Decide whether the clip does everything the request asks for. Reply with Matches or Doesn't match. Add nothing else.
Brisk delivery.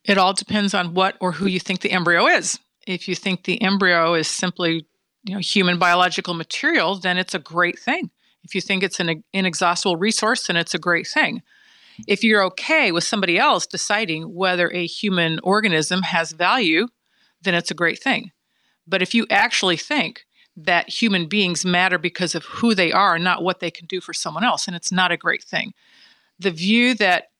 Doesn't match